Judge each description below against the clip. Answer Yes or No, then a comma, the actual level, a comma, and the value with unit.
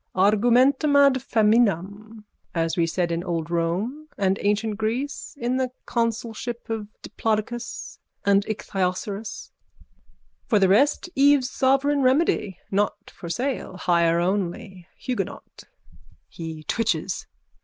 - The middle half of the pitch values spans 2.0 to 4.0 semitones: No, average, 5.1 semitones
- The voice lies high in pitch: Yes, high, 215 Hz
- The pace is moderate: No, slow, 110 wpm